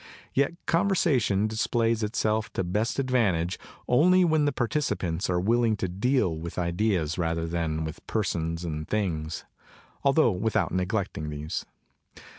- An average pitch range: No, wide, 6.3 semitones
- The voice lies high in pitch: No, low, 100 Hz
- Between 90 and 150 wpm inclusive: Yes, slow, 135 wpm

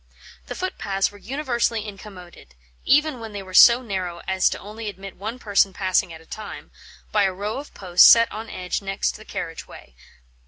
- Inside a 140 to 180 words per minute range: No, average, 190 wpm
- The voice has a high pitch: Yes, high, 205 Hz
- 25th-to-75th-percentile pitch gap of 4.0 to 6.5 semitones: No, average, 3.4 semitones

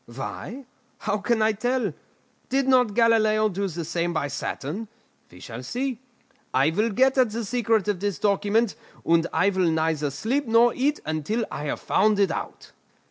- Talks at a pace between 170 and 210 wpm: Yes, average, 175 wpm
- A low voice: No, high, 210 Hz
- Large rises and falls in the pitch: Yes, wide, 5.9 semitones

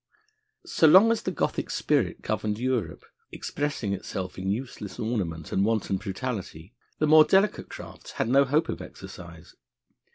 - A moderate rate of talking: Yes, average, 150 wpm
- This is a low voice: Yes, low, 115 Hz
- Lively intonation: Yes, wide, 7.2 semitones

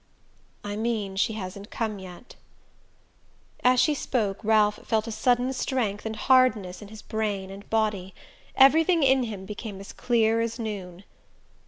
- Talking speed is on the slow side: No, average, 150 wpm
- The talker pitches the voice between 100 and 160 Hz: No, high, 220 Hz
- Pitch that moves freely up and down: No, average, 3.4 semitones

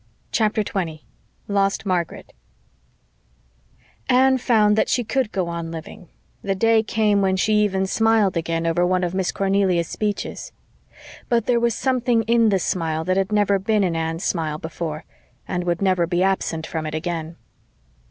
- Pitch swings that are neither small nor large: Yes, average, 4.0 semitones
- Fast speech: No, average, 160 wpm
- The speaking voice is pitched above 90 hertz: Yes, high, 190 Hz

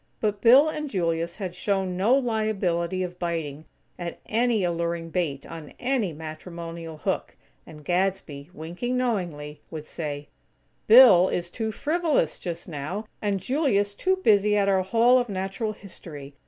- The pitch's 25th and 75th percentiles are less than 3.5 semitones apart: No, average, 4.8 semitones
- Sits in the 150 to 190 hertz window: Yes, medium, 185 Hz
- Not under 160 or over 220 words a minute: No, average, 145 wpm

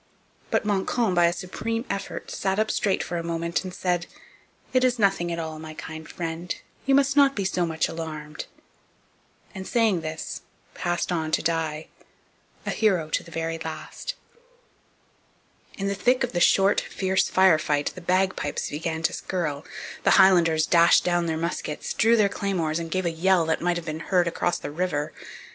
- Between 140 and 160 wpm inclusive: No, average, 180 wpm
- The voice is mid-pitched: Yes, medium, 175 Hz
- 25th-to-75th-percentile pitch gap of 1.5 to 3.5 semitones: Yes, average, 3.1 semitones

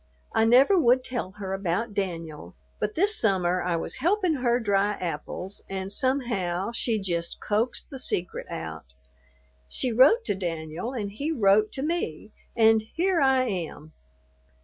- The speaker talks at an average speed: Yes, average, 150 wpm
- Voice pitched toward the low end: No, high, 210 Hz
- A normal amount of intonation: No, wide, 6.1 semitones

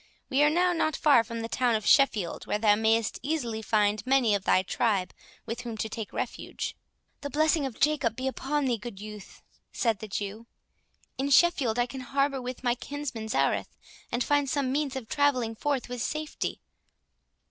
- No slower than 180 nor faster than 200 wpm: Yes, average, 185 wpm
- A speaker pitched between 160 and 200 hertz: No, high, 245 Hz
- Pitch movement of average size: Yes, average, 4.3 semitones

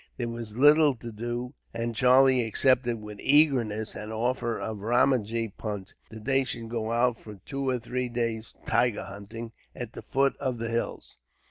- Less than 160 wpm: No, average, 170 wpm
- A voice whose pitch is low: Yes, low, 120 Hz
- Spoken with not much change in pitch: Yes, narrow, 2.3 semitones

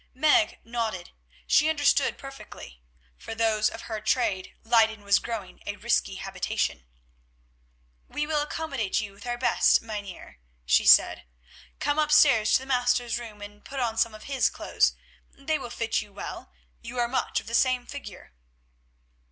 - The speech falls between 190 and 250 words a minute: No, average, 160 wpm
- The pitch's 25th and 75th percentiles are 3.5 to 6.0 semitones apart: Yes, average, 4.3 semitones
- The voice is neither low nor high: No, high, 235 Hz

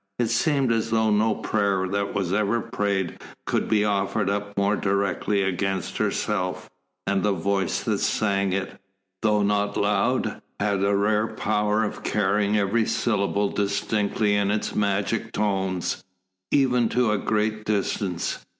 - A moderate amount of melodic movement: No, narrow, 1.5 semitones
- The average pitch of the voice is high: No, low, 105 Hz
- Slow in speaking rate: No, average, 145 wpm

